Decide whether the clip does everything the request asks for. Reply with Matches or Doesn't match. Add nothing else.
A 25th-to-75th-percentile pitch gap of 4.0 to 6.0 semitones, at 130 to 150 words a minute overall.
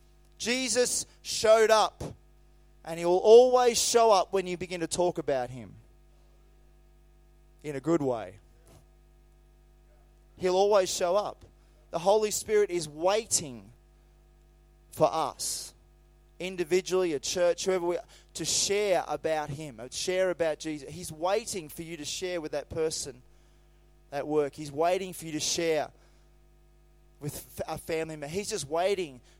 Doesn't match